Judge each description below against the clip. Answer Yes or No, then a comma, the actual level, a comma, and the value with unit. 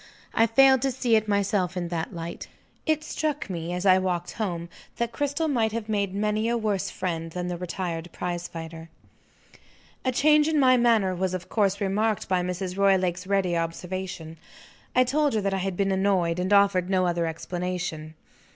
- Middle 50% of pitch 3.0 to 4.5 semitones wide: Yes, average, 3.9 semitones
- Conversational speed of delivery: Yes, average, 185 wpm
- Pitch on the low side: No, high, 190 Hz